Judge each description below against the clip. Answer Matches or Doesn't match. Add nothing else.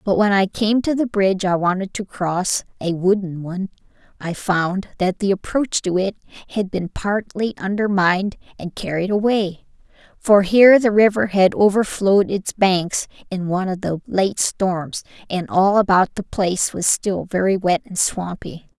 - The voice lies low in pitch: Doesn't match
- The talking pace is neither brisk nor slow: Matches